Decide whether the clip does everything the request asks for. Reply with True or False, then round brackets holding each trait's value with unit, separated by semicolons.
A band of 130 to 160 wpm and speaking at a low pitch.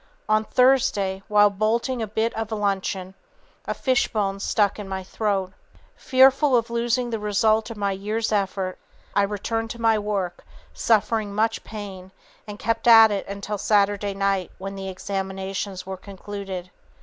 False (150 wpm; 205 Hz)